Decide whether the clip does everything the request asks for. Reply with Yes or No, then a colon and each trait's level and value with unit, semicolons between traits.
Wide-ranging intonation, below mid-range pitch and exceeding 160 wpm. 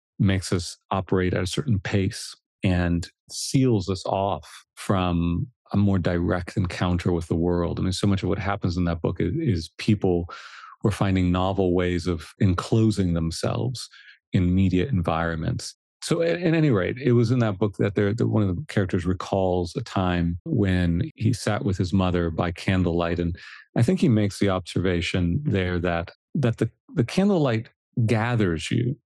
No: average, 3.6 semitones; very low, 95 Hz; average, 175 wpm